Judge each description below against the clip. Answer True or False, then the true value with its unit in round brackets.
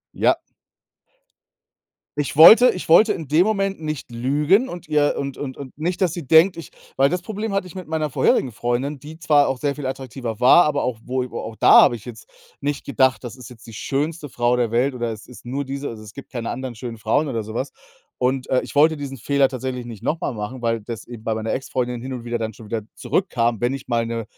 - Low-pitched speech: True (130 Hz)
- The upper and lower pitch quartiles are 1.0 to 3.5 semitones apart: False (4.2 semitones)